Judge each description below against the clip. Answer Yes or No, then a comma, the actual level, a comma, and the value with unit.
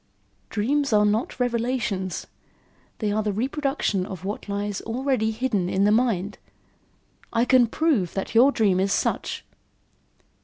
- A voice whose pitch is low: No, high, 220 Hz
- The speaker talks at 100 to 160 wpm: Yes, average, 140 wpm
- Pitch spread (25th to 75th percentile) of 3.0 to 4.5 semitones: Yes, average, 3.9 semitones